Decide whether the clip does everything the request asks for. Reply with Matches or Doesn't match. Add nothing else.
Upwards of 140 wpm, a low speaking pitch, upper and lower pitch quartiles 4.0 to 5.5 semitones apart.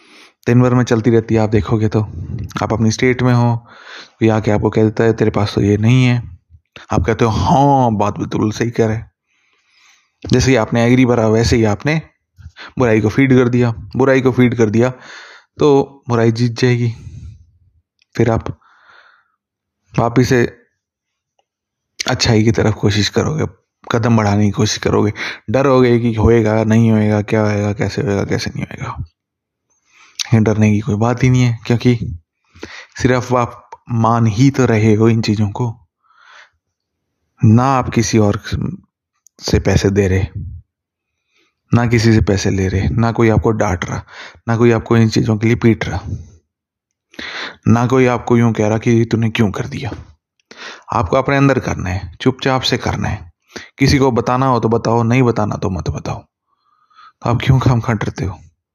Doesn't match